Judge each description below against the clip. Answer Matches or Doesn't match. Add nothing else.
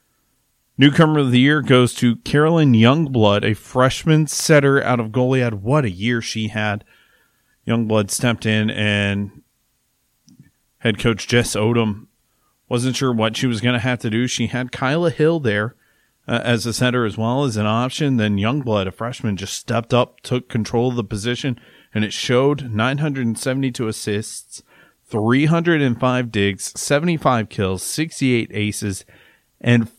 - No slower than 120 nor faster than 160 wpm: Matches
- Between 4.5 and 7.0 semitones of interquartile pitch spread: Doesn't match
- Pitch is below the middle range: Matches